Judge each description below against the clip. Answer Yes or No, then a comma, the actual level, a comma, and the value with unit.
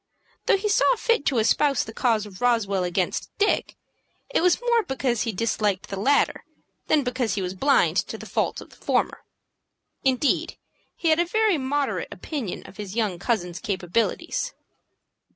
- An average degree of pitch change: No, wide, 6.7 semitones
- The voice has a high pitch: Yes, high, 245 Hz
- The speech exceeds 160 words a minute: Yes, average, 170 wpm